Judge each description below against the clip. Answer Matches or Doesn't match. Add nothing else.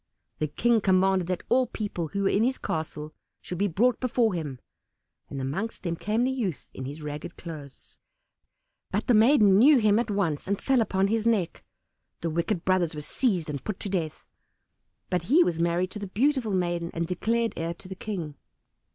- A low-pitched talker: Doesn't match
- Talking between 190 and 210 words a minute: Matches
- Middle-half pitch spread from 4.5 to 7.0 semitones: Matches